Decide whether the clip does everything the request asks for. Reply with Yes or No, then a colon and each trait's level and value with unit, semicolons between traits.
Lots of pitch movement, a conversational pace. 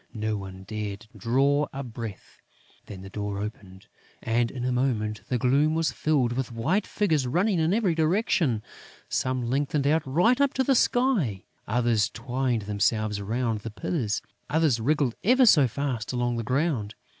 Yes: wide, 6.2 semitones; average, 165 wpm